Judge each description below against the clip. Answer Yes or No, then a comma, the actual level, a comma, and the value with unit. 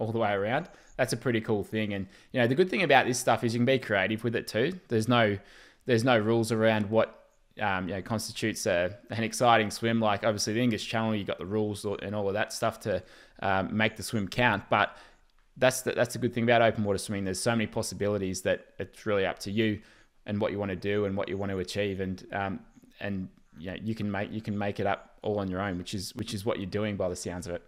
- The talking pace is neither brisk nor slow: No, fast, 265 wpm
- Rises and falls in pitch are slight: Yes, narrow, 2.2 semitones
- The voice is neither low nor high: No, low, 105 Hz